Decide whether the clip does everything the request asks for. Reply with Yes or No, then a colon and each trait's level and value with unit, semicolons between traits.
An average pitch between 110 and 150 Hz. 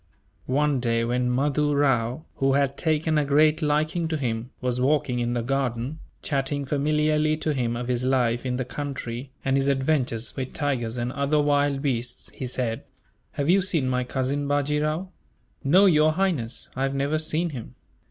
Yes: medium, 140 Hz